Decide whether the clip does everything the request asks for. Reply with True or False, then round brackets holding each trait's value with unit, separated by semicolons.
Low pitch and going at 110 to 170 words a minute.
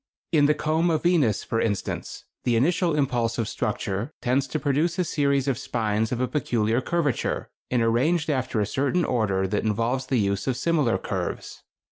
False (130 Hz; 180 wpm)